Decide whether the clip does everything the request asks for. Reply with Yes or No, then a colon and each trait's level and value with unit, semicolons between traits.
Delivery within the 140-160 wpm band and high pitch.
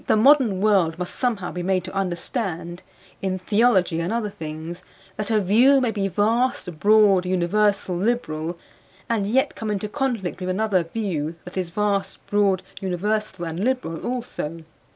Yes: average, 155 wpm; high, 195 Hz